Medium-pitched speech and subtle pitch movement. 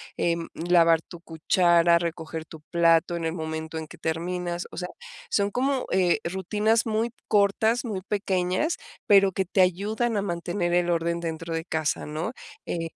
No: medium, 175 Hz; average, 3.1 semitones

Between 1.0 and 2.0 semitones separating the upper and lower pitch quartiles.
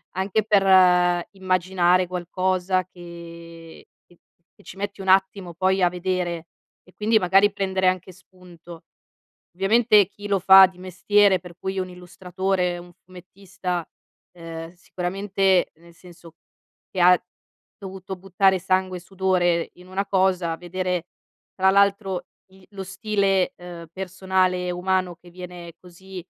Yes: narrow, 1.4 semitones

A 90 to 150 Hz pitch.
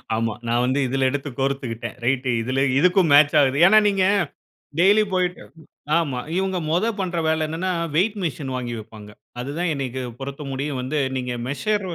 Yes: medium, 140 Hz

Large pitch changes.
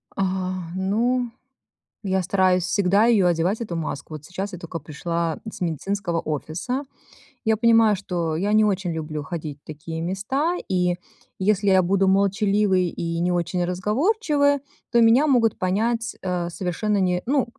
No: average, 3.8 semitones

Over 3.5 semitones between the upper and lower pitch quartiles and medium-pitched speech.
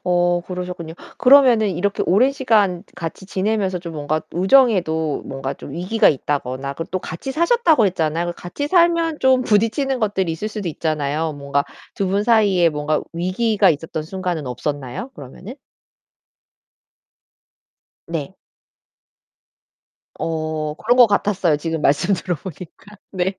Yes: wide, 5.4 semitones; medium, 180 Hz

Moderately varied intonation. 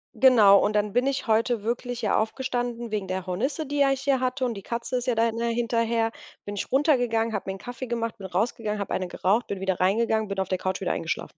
Yes: average, 3.3 semitones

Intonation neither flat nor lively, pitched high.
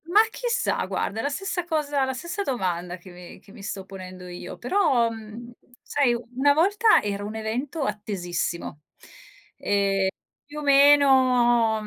No: wide, 6.4 semitones; high, 240 Hz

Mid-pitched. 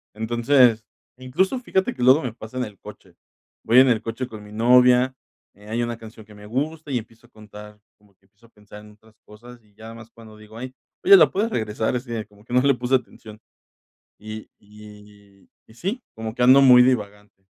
No: low, 115 Hz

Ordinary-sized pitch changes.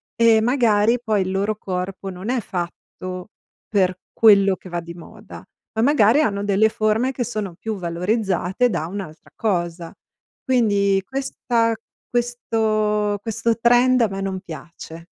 Yes: average, 3.7 semitones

